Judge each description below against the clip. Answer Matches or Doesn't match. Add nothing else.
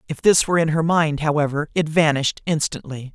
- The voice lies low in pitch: Doesn't match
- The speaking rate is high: Doesn't match